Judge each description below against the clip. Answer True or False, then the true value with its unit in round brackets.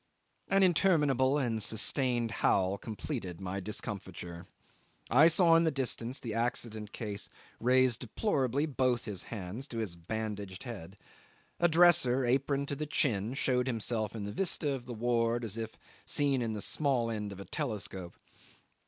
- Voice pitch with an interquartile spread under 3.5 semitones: False (4.6 semitones)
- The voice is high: False (120 Hz)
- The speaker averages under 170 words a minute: True (155 wpm)